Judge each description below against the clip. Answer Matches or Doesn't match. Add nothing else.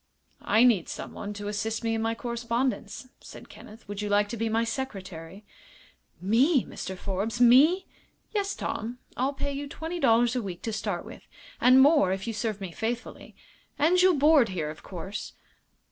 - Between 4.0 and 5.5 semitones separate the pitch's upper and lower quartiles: Matches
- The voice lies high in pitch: Matches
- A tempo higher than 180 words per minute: Doesn't match